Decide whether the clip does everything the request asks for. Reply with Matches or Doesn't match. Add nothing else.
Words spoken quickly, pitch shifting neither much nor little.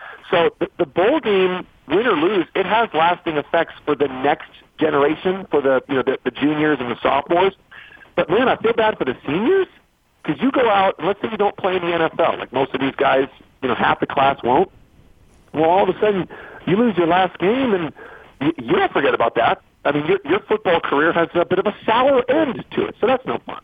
Doesn't match